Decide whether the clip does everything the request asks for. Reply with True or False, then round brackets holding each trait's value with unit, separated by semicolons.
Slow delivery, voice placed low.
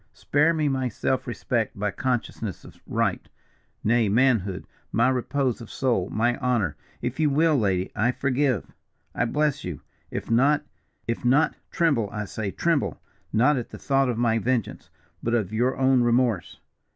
False (165 wpm; 120 Hz)